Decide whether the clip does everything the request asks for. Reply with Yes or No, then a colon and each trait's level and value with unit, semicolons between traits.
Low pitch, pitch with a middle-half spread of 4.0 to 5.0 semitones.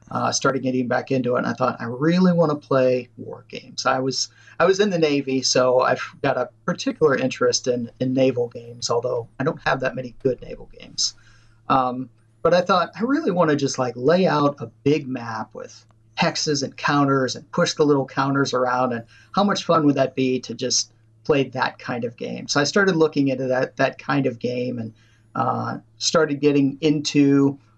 No: low, 130 Hz; average, 3.1 semitones